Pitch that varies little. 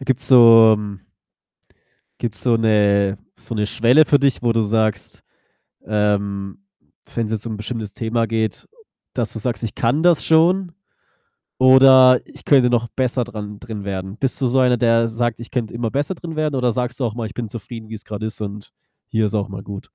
No: average, 3.1 semitones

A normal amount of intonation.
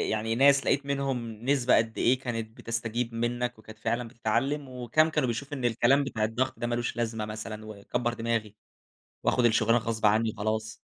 No: narrow, 2.3 semitones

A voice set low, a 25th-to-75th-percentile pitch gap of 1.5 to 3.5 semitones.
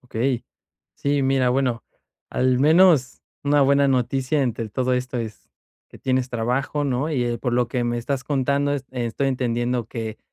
Yes: low, 130 Hz; narrow, 2.4 semitones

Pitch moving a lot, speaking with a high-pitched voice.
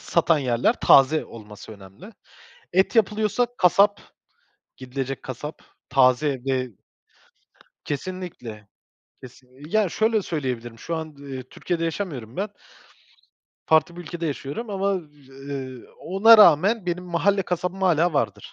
No: wide, 6.3 semitones; medium, 155 Hz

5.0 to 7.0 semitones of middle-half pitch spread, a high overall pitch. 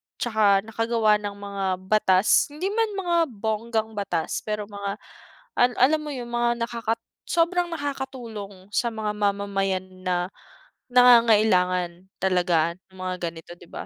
No: average, 4.0 semitones; high, 215 Hz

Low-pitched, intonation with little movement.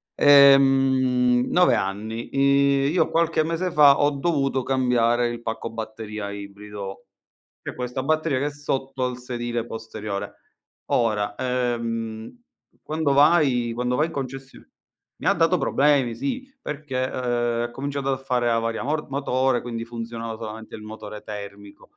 No: low, 125 Hz; average, 3.4 semitones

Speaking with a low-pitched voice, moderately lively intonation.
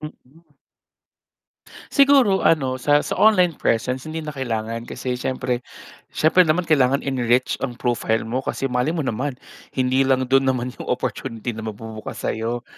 Yes: low, 130 Hz; average, 3.9 semitones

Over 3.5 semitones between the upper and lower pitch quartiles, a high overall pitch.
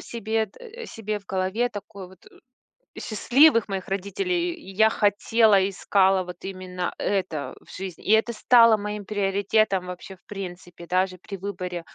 No: average, 2.9 semitones; high, 200 Hz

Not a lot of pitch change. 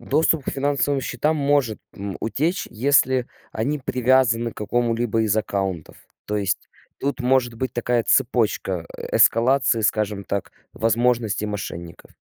No: average, 3.8 semitones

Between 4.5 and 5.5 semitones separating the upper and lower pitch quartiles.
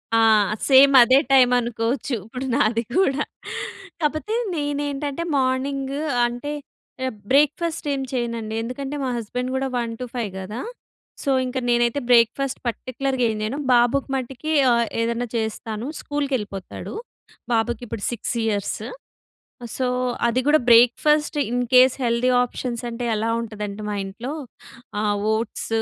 No: average, 3.0 semitones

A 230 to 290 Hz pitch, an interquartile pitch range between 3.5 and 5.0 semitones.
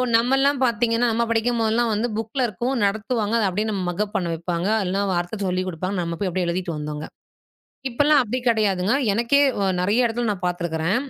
No: high, 210 Hz; average, 4.6 semitones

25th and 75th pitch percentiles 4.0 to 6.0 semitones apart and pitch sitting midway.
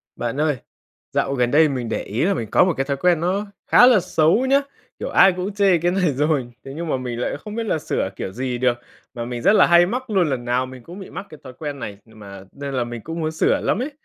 No: wide, 6.6 semitones; medium, 150 Hz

